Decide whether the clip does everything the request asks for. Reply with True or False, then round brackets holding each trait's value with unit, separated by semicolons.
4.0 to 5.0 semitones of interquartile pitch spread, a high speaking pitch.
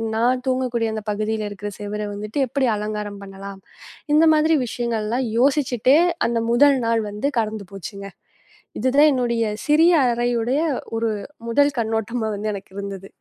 False (3.6 semitones; 230 Hz)